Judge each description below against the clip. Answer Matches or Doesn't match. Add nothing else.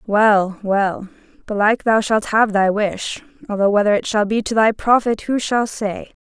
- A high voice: Matches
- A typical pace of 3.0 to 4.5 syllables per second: Matches